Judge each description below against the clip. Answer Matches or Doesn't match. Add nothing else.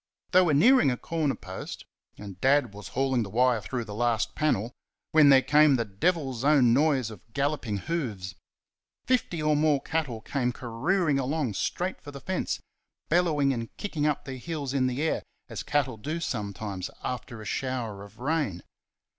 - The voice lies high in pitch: Doesn't match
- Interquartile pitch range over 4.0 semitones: Matches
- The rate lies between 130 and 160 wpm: Doesn't match